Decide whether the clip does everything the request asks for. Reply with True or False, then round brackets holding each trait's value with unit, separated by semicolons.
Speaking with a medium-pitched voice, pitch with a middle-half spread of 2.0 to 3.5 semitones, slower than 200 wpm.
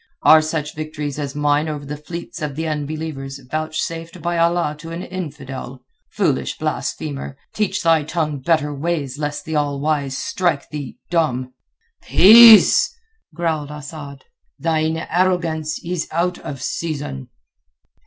True (155 Hz; 2.4 semitones; 135 wpm)